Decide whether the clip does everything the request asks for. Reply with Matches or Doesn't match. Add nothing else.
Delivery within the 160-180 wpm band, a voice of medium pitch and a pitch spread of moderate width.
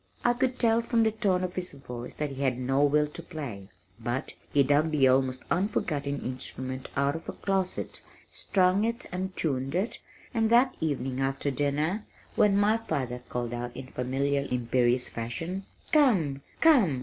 Doesn't match